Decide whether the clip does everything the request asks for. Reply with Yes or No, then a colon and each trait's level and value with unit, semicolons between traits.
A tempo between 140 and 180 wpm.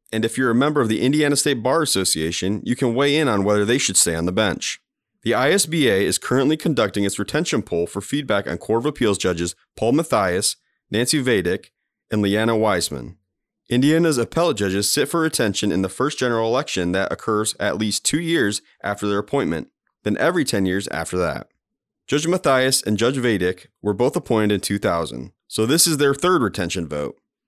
No: average, 190 wpm